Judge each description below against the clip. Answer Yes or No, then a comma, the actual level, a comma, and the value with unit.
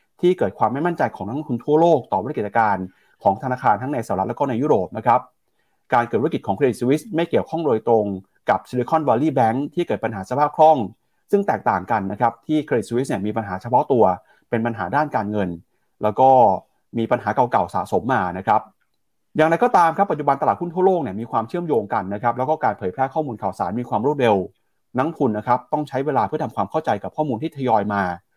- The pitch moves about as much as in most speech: No, wide, 5.7 semitones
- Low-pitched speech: Yes, low, 130 Hz